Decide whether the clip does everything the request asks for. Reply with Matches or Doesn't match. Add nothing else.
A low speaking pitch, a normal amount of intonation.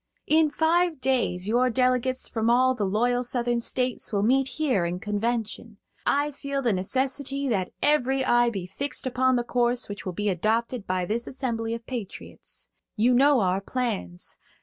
Doesn't match